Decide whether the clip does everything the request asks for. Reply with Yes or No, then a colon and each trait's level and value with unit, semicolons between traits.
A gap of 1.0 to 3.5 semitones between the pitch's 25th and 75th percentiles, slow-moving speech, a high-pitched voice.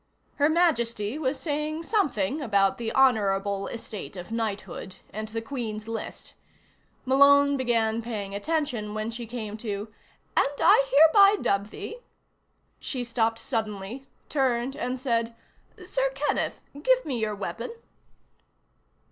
No: average, 4.7 semitones; slow, 130 wpm; high, 235 Hz